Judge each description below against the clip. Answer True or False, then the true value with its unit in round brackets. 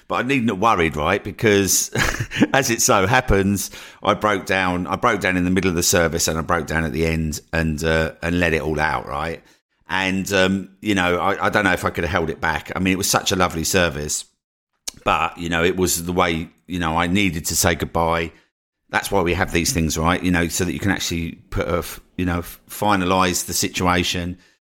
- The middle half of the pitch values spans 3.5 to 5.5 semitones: False (2.6 semitones)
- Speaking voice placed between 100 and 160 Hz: False (90 Hz)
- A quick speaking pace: True (235 wpm)